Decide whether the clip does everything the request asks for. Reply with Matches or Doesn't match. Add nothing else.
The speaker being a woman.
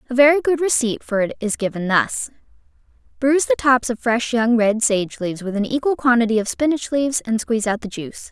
Matches